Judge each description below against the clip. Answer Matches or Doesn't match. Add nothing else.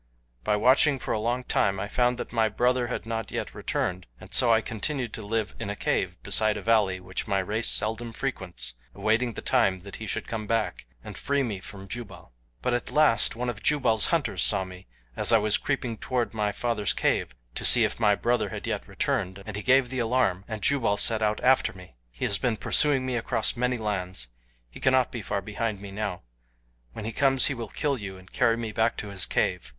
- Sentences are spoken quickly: Matches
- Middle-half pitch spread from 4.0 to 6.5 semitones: Doesn't match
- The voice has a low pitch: Matches